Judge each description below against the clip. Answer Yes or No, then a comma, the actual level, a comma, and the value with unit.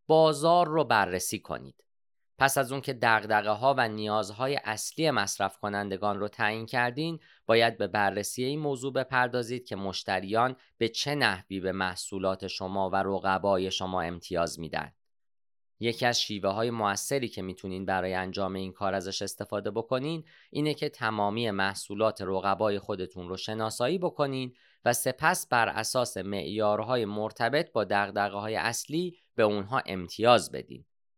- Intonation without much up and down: No, average, 4.5 semitones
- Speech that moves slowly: No, average, 140 wpm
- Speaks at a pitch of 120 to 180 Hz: No, low, 105 Hz